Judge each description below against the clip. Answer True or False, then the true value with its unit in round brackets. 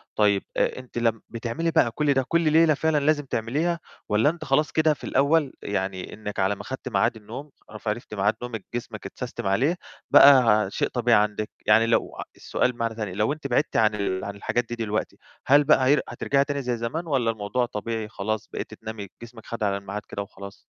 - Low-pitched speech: True (115 Hz)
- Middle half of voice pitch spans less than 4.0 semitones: False (4.8 semitones)